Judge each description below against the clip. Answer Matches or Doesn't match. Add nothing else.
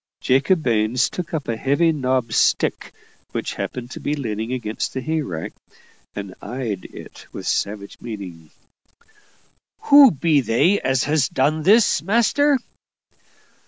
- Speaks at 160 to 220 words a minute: Doesn't match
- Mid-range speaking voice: Doesn't match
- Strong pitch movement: Matches